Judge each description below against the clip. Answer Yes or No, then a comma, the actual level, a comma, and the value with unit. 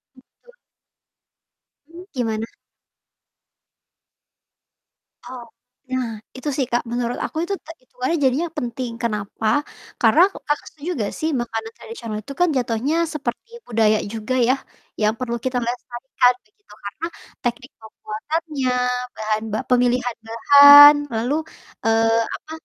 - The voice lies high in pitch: Yes, high, 245 Hz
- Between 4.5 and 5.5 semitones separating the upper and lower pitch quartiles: No, average, 4.1 semitones